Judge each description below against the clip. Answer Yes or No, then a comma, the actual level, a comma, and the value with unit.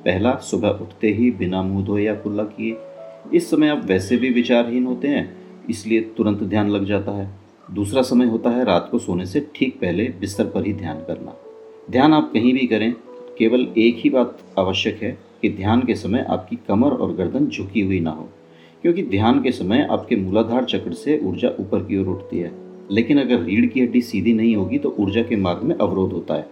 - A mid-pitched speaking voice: No, low, 110 Hz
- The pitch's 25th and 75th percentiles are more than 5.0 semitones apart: No, average, 3.9 semitones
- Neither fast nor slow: No, fast, 210 wpm